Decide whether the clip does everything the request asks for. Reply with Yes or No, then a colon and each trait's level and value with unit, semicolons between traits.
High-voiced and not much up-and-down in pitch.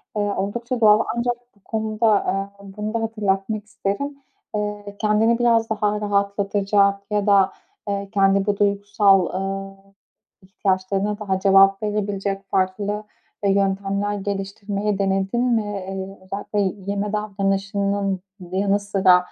Yes: high, 200 Hz; narrow, 1.3 semitones